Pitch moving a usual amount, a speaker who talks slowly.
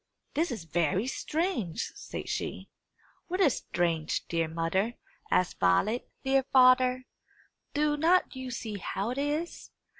No: wide, 8.7 semitones; slow, 130 wpm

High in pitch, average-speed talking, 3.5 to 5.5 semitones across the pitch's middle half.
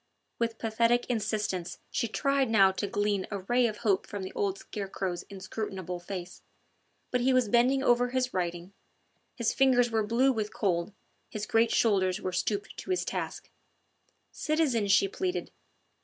Yes: high, 215 Hz; average, 155 wpm; average, 4.0 semitones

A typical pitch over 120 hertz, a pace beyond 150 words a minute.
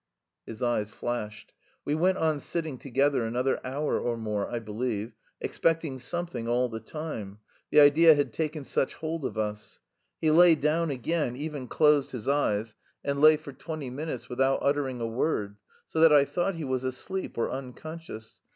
Yes: low, 135 Hz; average, 170 wpm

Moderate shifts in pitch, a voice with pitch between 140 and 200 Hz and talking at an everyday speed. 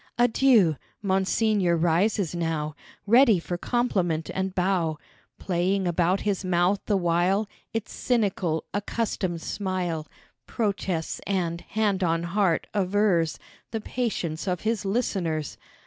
No: average, 3.4 semitones; medium, 185 Hz; slow, 115 wpm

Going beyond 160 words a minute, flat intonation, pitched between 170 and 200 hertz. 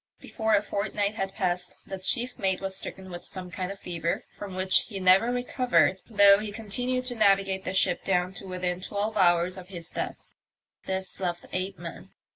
Yes: average, 190 wpm; narrow, 2.0 semitones; high, 190 Hz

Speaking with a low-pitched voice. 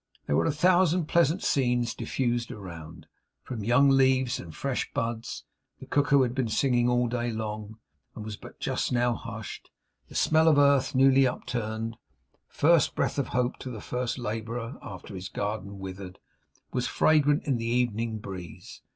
Yes: low, 120 Hz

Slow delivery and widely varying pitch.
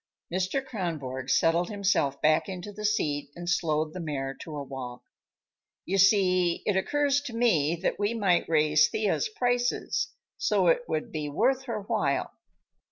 No: average, 160 wpm; wide, 6.3 semitones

